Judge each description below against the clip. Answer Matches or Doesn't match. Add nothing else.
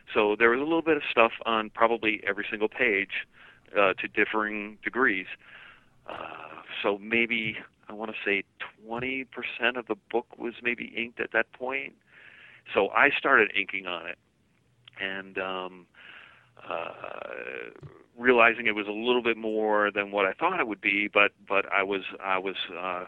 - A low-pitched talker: Matches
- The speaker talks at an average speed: Matches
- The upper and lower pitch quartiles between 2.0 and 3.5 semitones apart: Matches